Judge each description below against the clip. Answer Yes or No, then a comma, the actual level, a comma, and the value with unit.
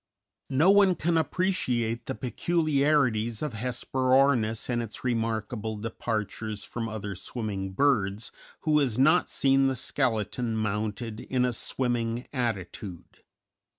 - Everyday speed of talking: No, slow, 120 wpm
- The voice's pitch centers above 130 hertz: No, low, 120 Hz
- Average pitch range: Yes, average, 3.8 semitones